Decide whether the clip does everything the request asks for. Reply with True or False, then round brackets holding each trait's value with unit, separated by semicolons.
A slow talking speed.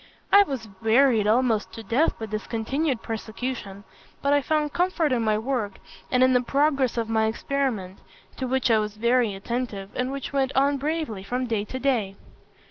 False (185 wpm)